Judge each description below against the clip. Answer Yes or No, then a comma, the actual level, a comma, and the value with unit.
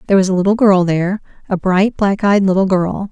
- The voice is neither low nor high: No, high, 195 Hz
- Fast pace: Yes, fast, 230 wpm